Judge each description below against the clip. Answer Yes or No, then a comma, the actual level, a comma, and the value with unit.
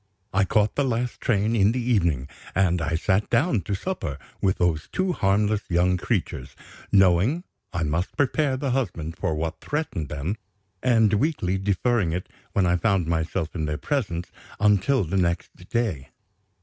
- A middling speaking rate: Yes, average, 160 wpm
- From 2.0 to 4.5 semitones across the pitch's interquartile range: No, wide, 5.6 semitones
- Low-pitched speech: Yes, very low, 95 Hz